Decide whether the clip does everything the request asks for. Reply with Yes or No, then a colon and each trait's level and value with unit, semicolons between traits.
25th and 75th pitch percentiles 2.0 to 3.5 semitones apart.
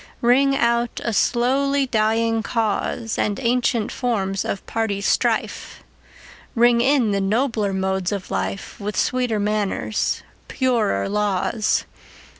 Yes: average, 3.2 semitones